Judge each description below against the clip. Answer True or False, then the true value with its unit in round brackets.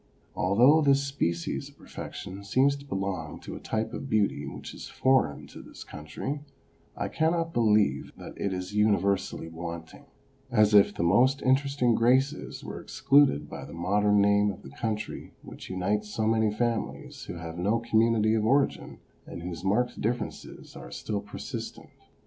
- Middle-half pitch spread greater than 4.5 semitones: True (4.9 semitones)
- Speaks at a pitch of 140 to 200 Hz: False (105 Hz)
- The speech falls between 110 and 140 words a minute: False (160 wpm)